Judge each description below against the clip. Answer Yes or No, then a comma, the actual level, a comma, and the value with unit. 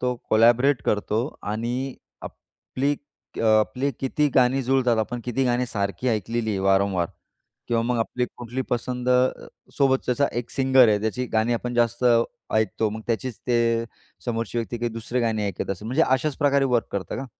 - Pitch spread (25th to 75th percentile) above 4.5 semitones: No, narrow, 2.6 semitones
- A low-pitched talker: Yes, low, 120 Hz